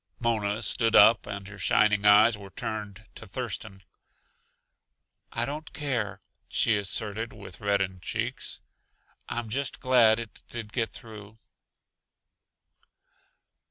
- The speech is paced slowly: Yes, slow, 115 wpm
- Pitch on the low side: Yes, low, 110 Hz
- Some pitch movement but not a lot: No, narrow, 2.3 semitones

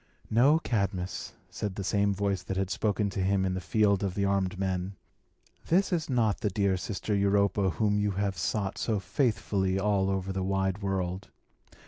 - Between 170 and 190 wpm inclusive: Yes, average, 180 wpm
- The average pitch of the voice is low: Yes, low, 100 Hz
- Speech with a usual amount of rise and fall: No, narrow, 1.4 semitones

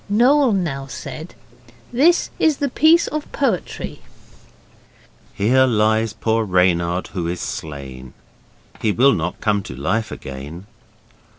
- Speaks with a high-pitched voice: No, low, 110 Hz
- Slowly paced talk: Yes, slow, 120 wpm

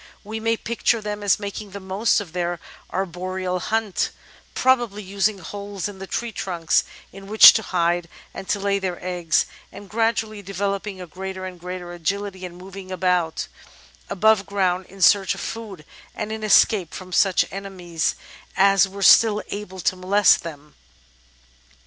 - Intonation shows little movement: Yes, narrow, 2.1 semitones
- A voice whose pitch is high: Yes, high, 195 Hz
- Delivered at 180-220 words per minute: No, average, 160 wpm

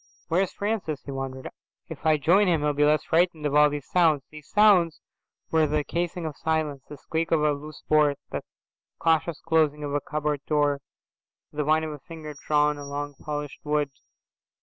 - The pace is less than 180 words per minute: No, average, 185 wpm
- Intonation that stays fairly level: Yes, narrow, 1.7 semitones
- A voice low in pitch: No, medium, 150 Hz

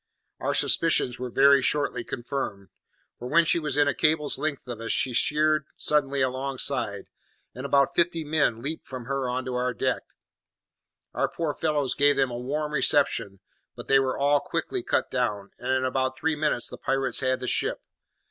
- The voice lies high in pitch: No, low, 135 Hz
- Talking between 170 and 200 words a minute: Yes, average, 185 wpm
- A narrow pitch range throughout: No, average, 3.0 semitones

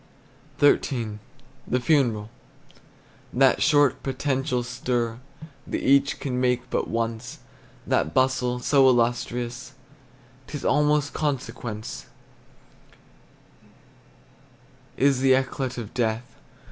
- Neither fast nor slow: No, slow, 95 wpm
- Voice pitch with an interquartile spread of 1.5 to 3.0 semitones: Yes, narrow, 2.5 semitones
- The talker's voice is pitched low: Yes, low, 125 Hz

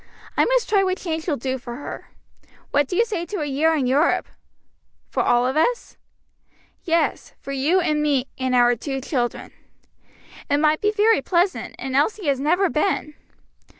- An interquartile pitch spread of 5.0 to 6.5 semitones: Yes, wide, 5.5 semitones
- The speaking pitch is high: Yes, very high, 305 Hz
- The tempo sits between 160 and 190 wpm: Yes, average, 180 wpm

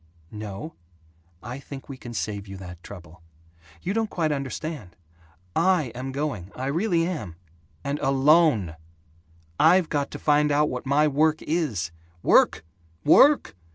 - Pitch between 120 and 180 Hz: Yes, medium, 140 Hz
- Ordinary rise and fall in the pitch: No, wide, 6.8 semitones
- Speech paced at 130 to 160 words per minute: Yes, average, 145 wpm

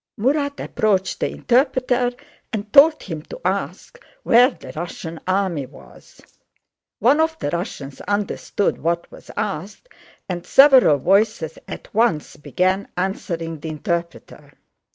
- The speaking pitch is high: Yes, high, 195 Hz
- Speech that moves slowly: Yes, slow, 125 wpm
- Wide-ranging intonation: Yes, wide, 6.8 semitones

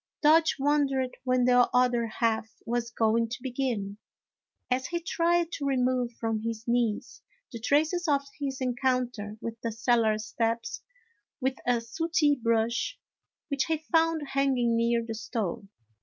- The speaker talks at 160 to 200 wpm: No, average, 140 wpm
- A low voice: No, high, 245 Hz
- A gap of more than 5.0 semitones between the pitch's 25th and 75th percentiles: No, average, 3.2 semitones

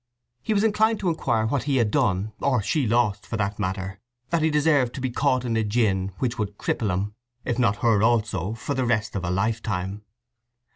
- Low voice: Yes, low, 115 Hz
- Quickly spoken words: Yes, fast, 210 wpm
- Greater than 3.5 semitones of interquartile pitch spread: Yes, average, 4.3 semitones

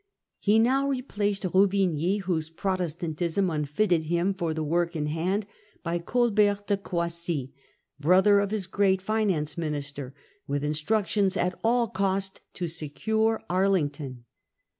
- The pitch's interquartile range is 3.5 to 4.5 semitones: Yes, average, 4.2 semitones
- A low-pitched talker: No, medium, 185 Hz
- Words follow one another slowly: Yes, slow, 130 wpm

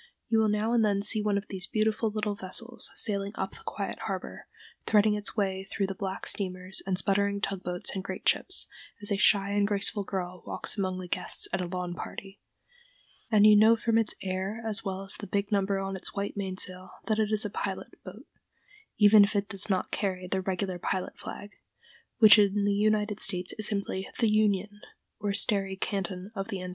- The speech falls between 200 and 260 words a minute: Yes, fast, 205 wpm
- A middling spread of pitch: No, narrow, 1.8 semitones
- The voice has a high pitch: Yes, high, 200 Hz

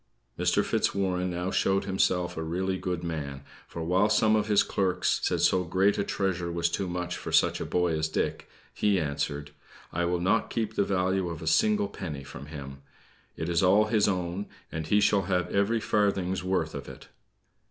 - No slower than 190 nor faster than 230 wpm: Yes, average, 195 wpm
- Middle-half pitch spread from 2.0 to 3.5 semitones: Yes, average, 2.7 semitones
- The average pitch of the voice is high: No, very low, 90 Hz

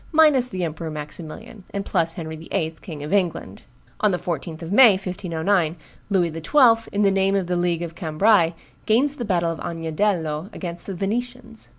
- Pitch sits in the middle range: Yes, medium, 180 Hz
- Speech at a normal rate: Yes, average, 180 wpm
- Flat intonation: No, average, 4.1 semitones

